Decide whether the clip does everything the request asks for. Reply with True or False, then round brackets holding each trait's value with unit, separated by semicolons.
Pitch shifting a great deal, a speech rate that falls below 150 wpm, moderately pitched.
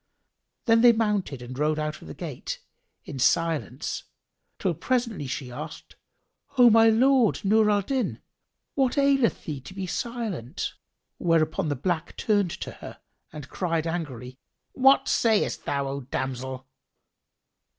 True (8.3 semitones; 140 wpm; 175 Hz)